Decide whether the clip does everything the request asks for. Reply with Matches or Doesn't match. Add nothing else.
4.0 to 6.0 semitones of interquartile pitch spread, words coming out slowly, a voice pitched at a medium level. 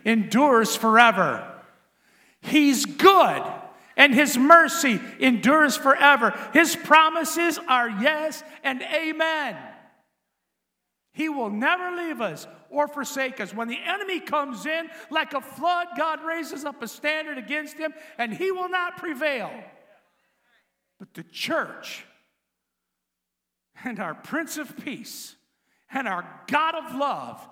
Doesn't match